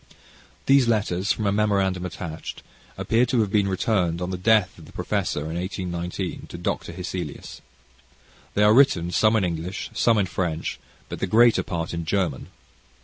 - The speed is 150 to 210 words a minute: Yes, average, 170 wpm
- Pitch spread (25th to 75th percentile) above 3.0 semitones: Yes, average, 3.7 semitones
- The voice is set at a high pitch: No, very low, 95 Hz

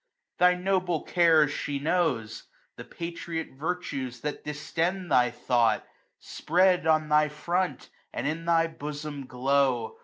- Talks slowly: Yes, slow, 125 wpm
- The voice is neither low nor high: Yes, medium, 155 Hz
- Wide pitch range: No, average, 3.9 semitones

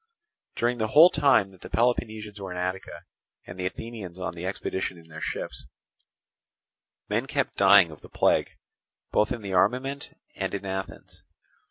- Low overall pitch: Yes, low, 100 Hz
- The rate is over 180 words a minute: No, average, 165 wpm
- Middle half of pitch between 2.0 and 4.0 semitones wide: No, average, 4.4 semitones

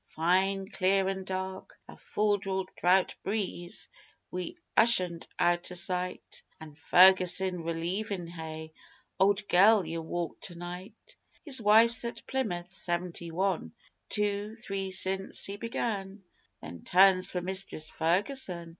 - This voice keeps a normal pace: No, slow, 125 wpm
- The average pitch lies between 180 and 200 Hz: Yes, high, 190 Hz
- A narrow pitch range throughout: Yes, narrow, 2.3 semitones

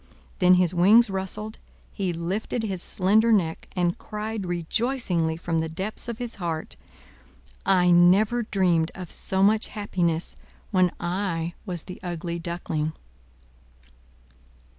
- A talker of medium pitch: Yes, medium, 180 Hz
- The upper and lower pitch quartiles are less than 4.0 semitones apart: Yes, average, 3.6 semitones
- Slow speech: Yes, slow, 125 wpm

